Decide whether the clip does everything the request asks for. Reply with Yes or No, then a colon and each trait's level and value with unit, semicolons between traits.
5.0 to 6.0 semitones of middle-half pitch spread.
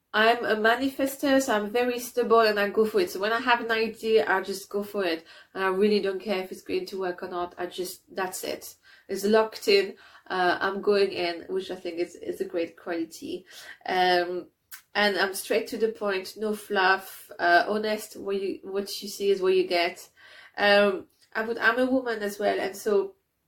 No: average, 3.3 semitones